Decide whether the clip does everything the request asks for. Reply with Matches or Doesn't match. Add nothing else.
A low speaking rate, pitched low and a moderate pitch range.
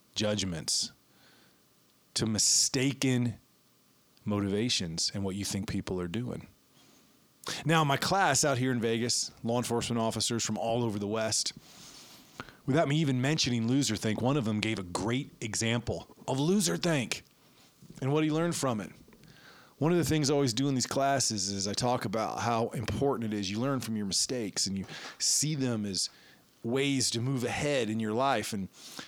Doesn't match